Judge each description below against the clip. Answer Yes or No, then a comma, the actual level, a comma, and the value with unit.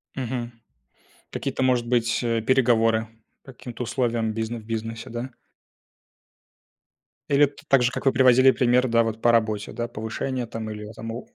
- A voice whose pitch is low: Yes, low, 120 Hz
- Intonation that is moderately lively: No, narrow, 2.1 semitones